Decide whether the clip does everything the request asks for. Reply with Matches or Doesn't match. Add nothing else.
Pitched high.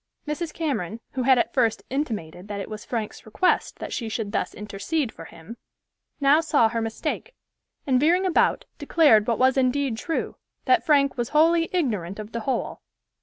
Matches